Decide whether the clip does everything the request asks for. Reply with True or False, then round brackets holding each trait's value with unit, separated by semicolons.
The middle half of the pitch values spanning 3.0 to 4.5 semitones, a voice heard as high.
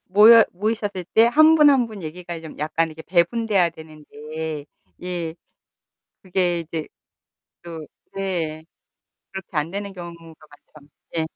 False (3.9 semitones; 175 Hz)